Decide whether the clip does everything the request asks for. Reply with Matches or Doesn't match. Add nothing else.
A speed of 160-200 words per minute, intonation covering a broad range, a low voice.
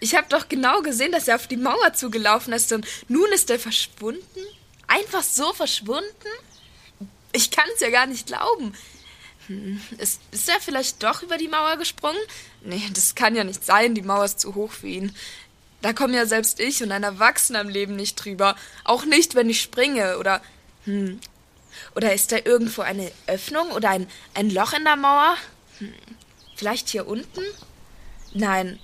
Doesn't match